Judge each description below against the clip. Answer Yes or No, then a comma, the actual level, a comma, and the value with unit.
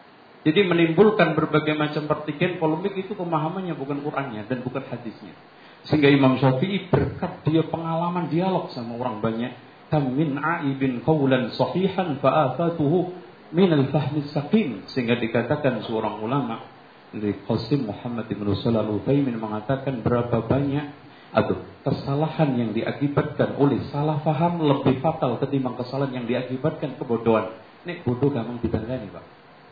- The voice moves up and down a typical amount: Yes, average, 4.5 semitones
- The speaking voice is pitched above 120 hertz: Yes, medium, 140 Hz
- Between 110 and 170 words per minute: Yes, average, 125 wpm